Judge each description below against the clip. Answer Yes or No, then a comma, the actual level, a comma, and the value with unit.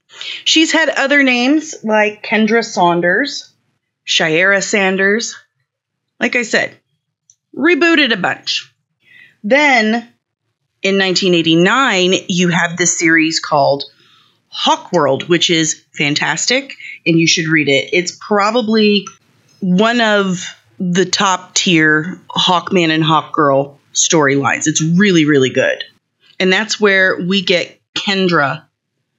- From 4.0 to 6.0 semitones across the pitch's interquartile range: Yes, wide, 5.5 semitones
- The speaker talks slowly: Yes, slow, 115 wpm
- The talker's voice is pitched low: No, medium, 180 Hz